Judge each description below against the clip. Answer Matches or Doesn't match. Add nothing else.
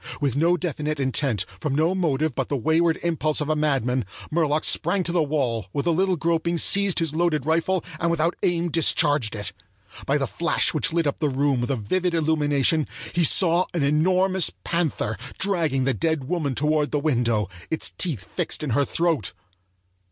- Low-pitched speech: Doesn't match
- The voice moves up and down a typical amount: Matches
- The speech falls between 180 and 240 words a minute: Matches